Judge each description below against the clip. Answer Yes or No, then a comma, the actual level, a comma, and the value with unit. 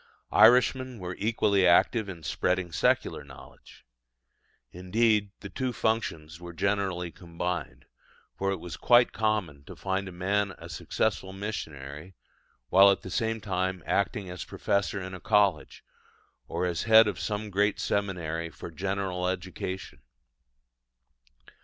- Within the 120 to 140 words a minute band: Yes, slow, 135 wpm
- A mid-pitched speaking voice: No, very low, 95 Hz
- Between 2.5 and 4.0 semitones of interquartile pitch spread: Yes, average, 2.8 semitones